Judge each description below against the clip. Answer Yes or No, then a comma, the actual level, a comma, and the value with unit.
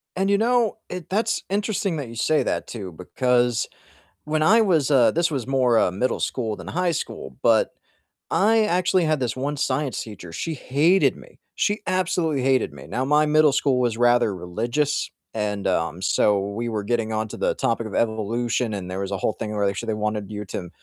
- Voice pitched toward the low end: Yes, low, 125 Hz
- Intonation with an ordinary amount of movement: No, wide, 6.7 semitones